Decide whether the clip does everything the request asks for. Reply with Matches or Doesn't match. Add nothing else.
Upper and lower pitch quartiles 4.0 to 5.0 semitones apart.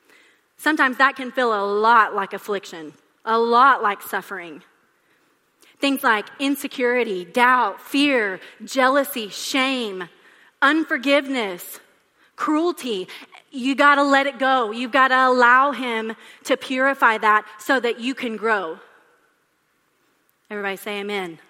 Matches